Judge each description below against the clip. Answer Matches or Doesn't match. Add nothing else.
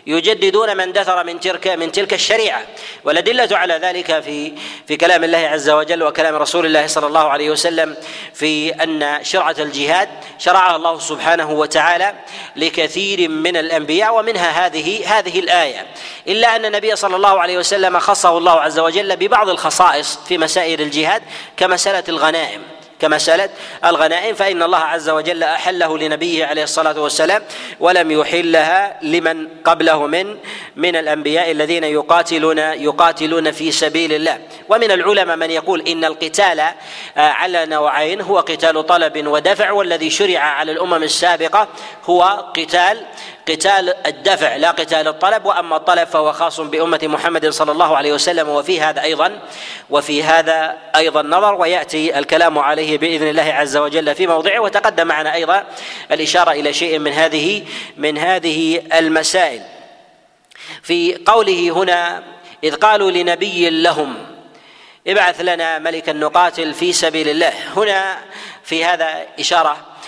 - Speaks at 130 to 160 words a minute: Matches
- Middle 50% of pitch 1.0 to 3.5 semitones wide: Matches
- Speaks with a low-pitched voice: Doesn't match